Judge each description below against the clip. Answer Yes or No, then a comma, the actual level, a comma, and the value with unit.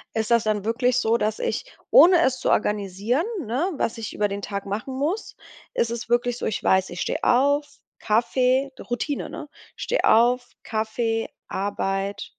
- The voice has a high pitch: Yes, high, 230 Hz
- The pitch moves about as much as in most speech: Yes, average, 3.5 semitones